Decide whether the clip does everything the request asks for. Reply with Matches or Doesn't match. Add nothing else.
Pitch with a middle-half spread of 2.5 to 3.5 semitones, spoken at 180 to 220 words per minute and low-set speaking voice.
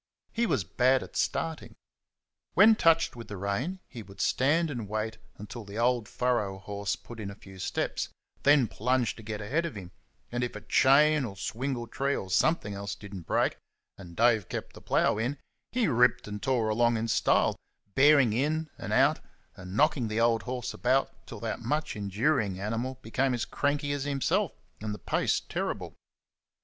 Doesn't match